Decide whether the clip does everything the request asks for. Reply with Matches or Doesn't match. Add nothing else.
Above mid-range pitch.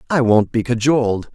Doesn't match